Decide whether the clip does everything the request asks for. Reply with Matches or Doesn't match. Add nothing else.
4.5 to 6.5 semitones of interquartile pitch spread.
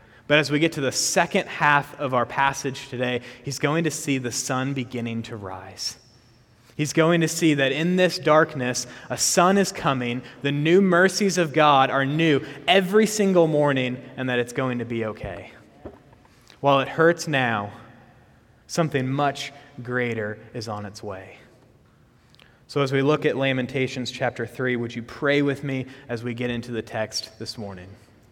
Doesn't match